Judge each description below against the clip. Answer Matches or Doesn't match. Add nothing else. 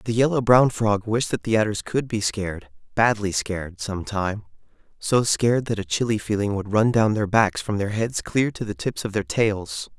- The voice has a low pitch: Matches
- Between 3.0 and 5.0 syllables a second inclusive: Matches